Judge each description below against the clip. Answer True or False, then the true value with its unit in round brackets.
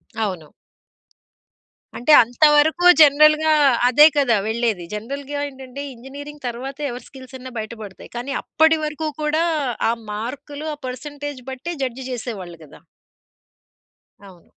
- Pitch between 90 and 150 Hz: False (265 Hz)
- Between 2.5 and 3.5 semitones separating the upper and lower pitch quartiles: False (4.1 semitones)